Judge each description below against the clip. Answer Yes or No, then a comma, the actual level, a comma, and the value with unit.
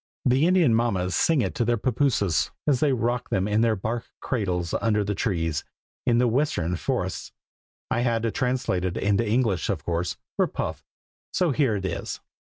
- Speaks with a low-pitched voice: Yes, low, 115 Hz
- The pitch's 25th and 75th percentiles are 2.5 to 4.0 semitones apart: No, average, 4.9 semitones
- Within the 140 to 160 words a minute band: No, average, 185 wpm